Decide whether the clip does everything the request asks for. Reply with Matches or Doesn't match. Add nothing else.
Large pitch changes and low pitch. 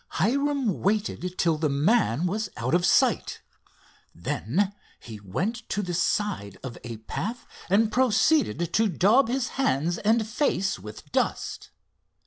Doesn't match